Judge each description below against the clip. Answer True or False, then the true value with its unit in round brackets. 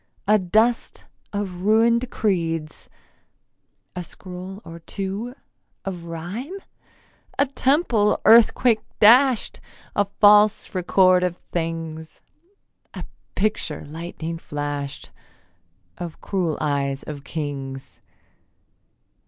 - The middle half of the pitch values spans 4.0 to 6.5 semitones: True (4.8 semitones)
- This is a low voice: False (185 Hz)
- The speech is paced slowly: True (90 wpm)